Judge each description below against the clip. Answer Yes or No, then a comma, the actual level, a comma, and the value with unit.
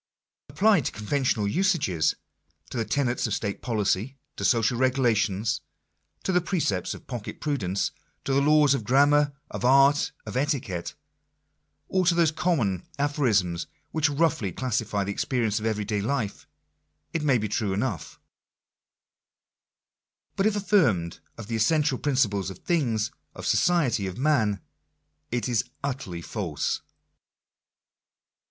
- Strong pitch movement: Yes, wide, 6.1 semitones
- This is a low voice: Yes, low, 120 Hz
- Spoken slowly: No, average, 145 wpm